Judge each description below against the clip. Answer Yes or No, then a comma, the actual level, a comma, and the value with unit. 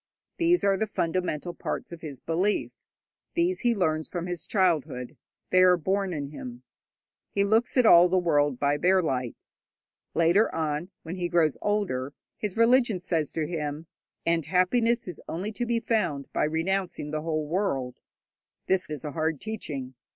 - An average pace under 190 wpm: Yes, average, 165 wpm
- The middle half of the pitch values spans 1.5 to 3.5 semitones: No, average, 4.7 semitones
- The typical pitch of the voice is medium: Yes, medium, 175 Hz